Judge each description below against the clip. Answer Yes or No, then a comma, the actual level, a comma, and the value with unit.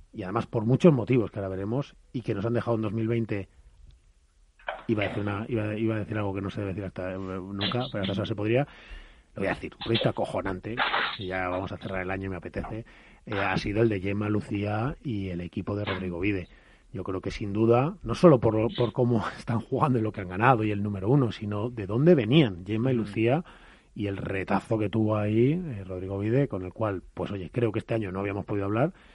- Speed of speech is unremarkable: No, fast, 235 wpm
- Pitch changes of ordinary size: Yes, average, 3.2 semitones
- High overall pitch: No, low, 105 Hz